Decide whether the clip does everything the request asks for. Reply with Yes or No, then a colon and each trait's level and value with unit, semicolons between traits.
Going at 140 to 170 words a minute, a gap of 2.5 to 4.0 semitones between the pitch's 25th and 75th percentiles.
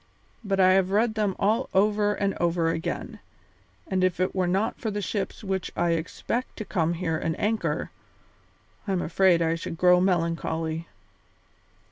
Yes: average, 165 wpm; average, 3.4 semitones